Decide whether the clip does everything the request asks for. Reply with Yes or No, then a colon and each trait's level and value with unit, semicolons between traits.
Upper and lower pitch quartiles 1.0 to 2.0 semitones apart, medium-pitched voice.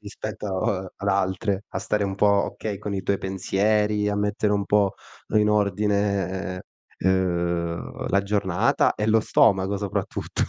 No: narrow, 1.7 semitones; low, 100 Hz